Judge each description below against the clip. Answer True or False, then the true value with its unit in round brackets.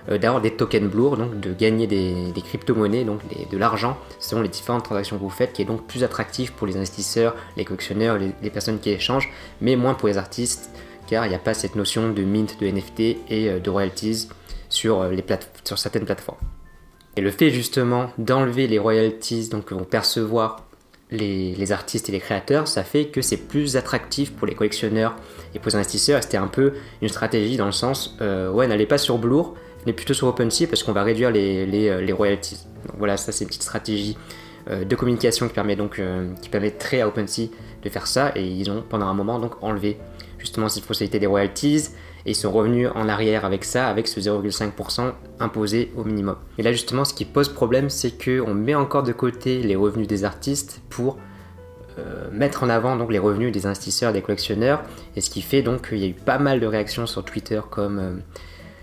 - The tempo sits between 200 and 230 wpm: True (215 wpm)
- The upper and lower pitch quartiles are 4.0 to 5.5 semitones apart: False (3.3 semitones)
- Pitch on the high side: False (110 Hz)